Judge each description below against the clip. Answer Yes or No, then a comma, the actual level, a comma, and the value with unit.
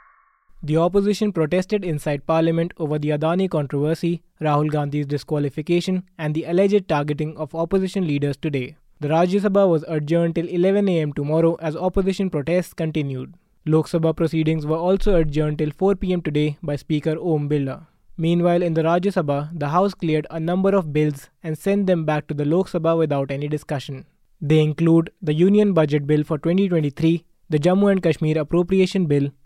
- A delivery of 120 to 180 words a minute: Yes, average, 170 wpm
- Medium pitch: Yes, medium, 160 Hz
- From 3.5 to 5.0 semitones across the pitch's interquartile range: No, average, 3.0 semitones